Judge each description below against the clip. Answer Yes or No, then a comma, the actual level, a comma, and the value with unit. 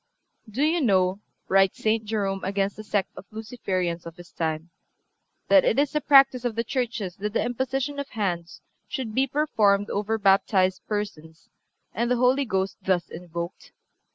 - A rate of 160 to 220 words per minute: Yes, average, 165 wpm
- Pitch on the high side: Yes, high, 210 Hz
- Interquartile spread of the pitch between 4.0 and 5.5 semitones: Yes, average, 4.9 semitones